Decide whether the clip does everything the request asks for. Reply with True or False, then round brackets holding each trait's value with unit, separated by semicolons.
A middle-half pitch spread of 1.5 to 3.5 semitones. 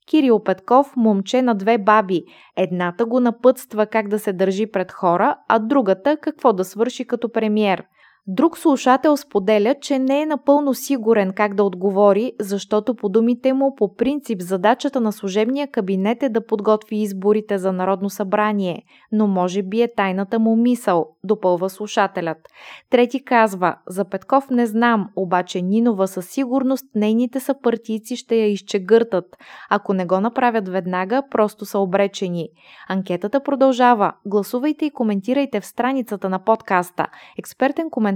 False (4.1 semitones)